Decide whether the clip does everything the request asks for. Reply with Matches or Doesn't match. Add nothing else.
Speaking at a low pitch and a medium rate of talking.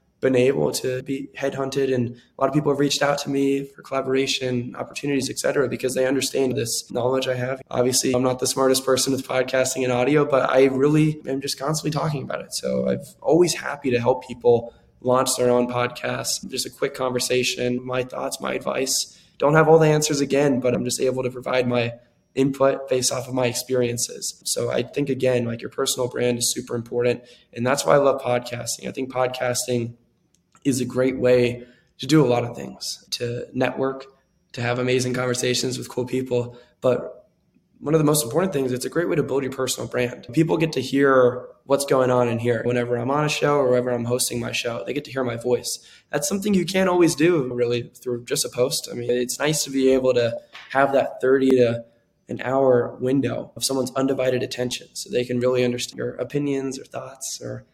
Doesn't match